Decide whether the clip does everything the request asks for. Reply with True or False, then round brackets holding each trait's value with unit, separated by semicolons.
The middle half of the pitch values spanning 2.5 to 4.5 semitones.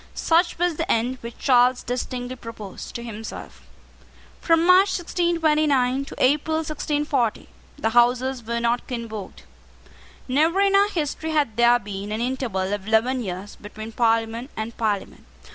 False (5.1 semitones)